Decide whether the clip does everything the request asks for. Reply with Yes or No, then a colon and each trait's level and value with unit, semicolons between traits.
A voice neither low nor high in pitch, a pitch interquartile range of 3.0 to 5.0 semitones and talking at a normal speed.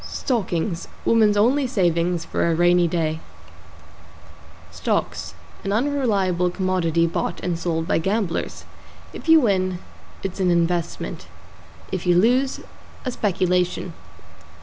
No: medium, 180 Hz; average, 3.6 semitones; slow, 115 wpm